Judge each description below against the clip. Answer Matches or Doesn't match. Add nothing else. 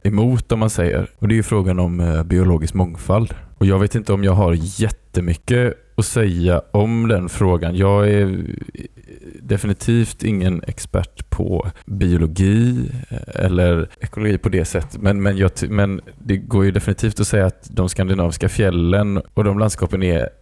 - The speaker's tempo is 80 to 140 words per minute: Doesn't match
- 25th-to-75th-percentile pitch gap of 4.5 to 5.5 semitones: Doesn't match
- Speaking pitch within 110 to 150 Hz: Doesn't match